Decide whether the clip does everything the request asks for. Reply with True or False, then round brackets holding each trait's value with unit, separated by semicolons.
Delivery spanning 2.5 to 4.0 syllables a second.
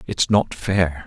True (3.2 syllables/s)